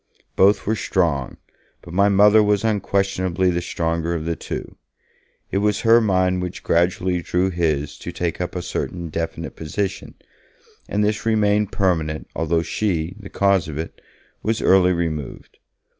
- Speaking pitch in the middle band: No, very low, 90 Hz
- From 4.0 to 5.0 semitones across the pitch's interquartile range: No, average, 3.3 semitones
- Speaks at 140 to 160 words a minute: Yes, average, 155 wpm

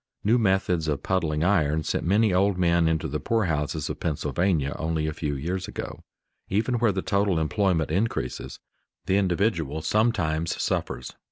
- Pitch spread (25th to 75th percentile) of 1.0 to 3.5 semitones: No, average, 4.2 semitones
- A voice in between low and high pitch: No, very low, 85 Hz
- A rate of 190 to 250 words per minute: No, average, 155 wpm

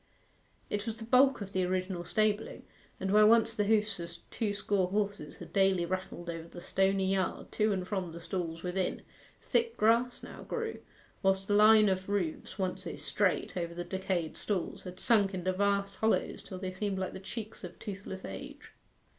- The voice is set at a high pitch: Yes, high, 195 Hz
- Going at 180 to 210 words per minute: Yes, average, 190 wpm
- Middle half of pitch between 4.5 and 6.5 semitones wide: No, narrow, 2.5 semitones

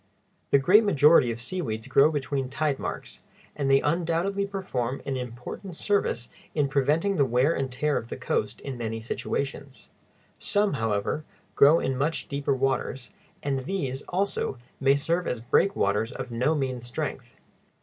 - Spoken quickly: No, average, 155 wpm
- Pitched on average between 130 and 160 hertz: Yes, medium, 140 Hz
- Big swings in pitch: No, average, 4.5 semitones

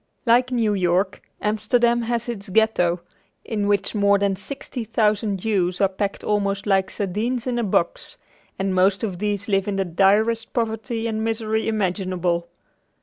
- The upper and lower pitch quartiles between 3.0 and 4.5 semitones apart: No, narrow, 2.6 semitones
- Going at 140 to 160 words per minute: Yes, average, 155 wpm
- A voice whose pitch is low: No, high, 205 Hz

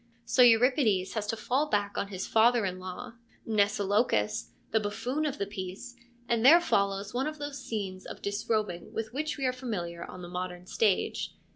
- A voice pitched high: Yes, high, 215 Hz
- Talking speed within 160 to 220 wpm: Yes, average, 180 wpm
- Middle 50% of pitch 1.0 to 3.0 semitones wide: No, average, 4.6 semitones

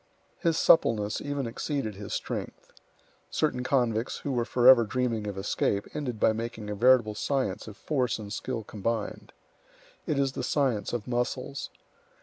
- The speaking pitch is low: Yes, low, 120 Hz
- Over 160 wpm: No, average, 150 wpm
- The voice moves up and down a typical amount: Yes, average, 3.6 semitones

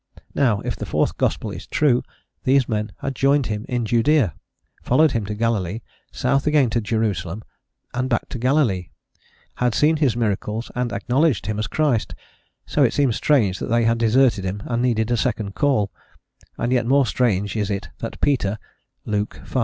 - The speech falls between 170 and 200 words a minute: Yes, average, 180 wpm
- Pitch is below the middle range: Yes, low, 115 Hz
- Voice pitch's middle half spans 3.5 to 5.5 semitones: Yes, average, 3.8 semitones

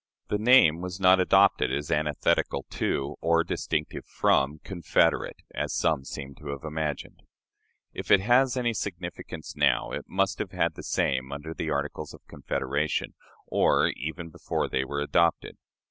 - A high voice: No, very low, 80 Hz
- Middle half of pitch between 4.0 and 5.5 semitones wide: Yes, average, 4.5 semitones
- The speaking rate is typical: Yes, average, 155 wpm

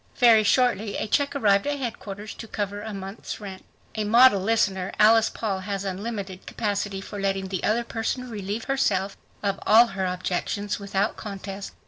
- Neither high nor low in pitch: No, high, 205 Hz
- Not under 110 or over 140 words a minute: No, average, 165 wpm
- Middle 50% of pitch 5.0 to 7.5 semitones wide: No, narrow, 2.4 semitones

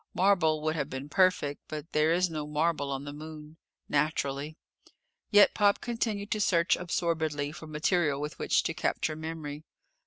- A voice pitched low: No, medium, 155 Hz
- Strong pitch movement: No, average, 2.8 semitones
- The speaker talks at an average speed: Yes, average, 160 wpm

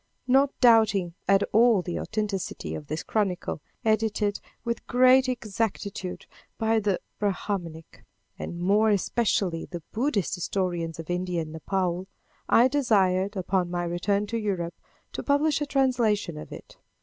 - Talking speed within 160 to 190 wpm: No, slow, 135 wpm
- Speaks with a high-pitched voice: Yes, high, 200 Hz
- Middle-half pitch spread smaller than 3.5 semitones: No, average, 4.2 semitones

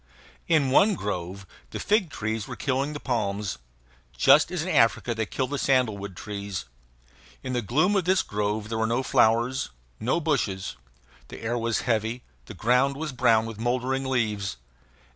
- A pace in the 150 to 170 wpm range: Yes, average, 165 wpm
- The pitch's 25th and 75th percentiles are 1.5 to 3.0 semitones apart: No, average, 4.1 semitones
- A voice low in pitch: Yes, low, 120 Hz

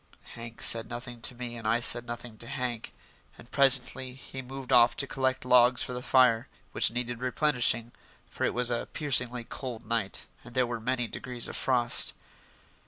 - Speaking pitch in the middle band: No, low, 125 Hz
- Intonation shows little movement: Yes, narrow, 1.4 semitones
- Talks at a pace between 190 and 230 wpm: No, average, 180 wpm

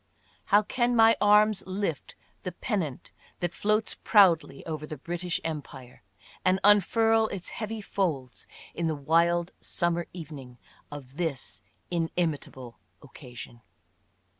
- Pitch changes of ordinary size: No, wide, 5.8 semitones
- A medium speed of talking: No, slow, 115 wpm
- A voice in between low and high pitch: Yes, medium, 170 Hz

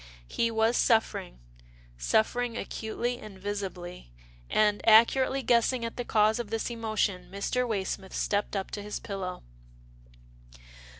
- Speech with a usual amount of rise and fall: Yes, average, 3.0 semitones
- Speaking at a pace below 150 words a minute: Yes, slow, 135 wpm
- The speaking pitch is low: No, high, 215 Hz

